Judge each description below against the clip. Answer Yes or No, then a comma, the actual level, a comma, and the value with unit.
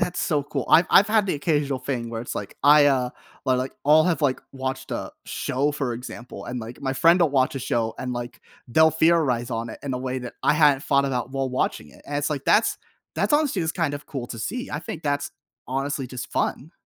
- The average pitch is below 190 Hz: Yes, medium, 140 Hz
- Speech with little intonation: No, average, 3.4 semitones